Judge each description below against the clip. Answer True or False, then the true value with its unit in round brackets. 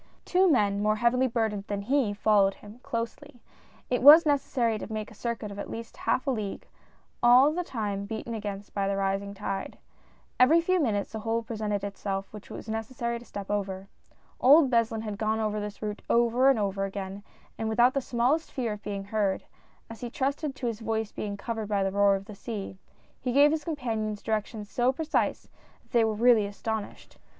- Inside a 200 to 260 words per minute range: True (205 wpm)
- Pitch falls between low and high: False (220 Hz)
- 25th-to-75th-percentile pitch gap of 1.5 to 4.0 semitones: True (3.3 semitones)